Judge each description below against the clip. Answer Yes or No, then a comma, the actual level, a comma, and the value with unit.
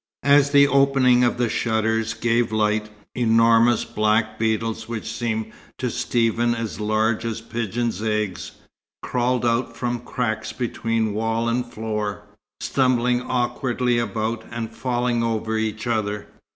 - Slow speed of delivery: Yes, slow, 130 wpm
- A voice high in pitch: No, low, 115 Hz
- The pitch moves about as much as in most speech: No, narrow, 1.6 semitones